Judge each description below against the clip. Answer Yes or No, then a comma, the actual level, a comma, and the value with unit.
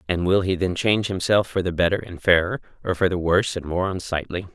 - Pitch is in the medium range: No, very low, 90 Hz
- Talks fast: Yes, fast, 240 wpm